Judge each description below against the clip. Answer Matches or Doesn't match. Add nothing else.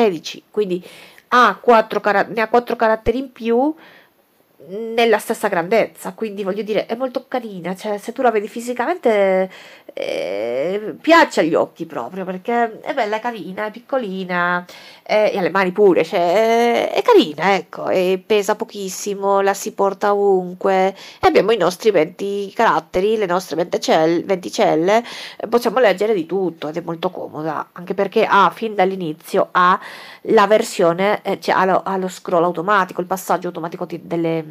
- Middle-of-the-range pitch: Doesn't match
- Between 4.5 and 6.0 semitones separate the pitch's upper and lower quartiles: Doesn't match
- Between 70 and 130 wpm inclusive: Doesn't match